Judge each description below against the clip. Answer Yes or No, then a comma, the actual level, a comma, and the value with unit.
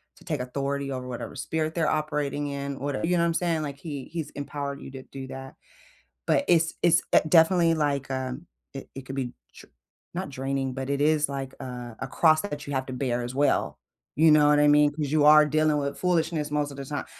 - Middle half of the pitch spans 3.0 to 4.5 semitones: No, narrow, 2.5 semitones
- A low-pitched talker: No, medium, 145 Hz